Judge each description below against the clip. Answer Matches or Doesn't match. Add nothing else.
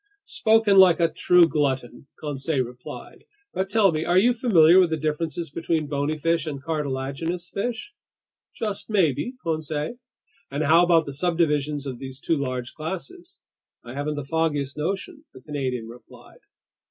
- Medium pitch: Matches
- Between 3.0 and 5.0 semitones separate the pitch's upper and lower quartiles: Matches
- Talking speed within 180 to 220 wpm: Doesn't match